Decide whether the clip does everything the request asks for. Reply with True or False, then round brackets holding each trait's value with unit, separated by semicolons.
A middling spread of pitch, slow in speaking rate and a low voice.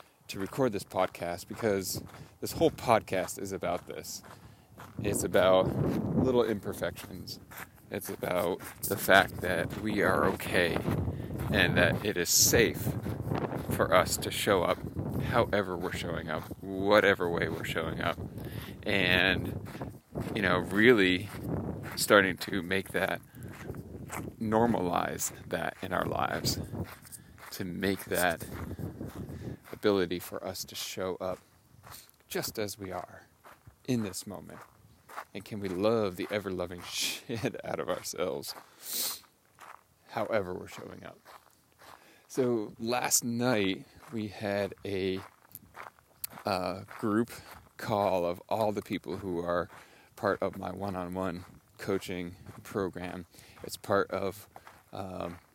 True (3.4 semitones; 120 wpm; 95 Hz)